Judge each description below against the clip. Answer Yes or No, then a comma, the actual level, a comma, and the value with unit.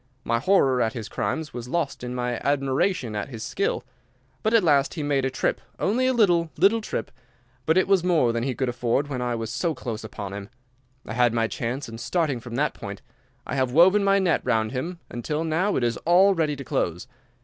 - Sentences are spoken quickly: Yes, fast, 215 wpm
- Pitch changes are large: Yes, wide, 6.2 semitones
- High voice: No, low, 135 Hz